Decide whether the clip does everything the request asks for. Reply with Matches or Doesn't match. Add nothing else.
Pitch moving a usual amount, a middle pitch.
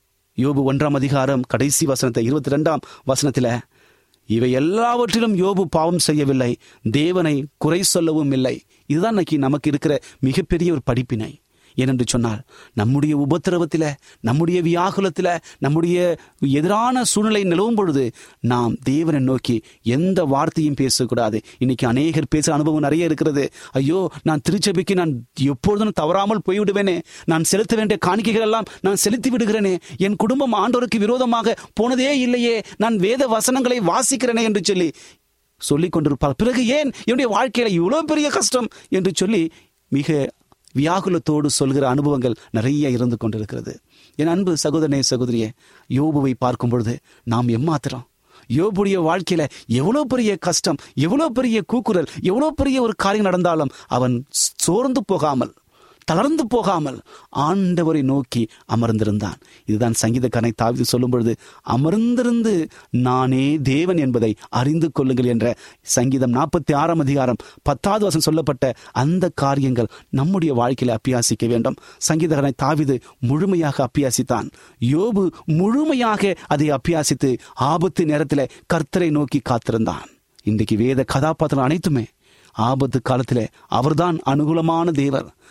Doesn't match